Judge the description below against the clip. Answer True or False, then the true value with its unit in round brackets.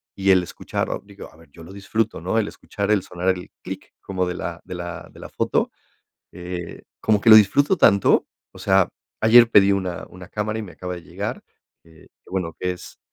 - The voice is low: True (95 Hz)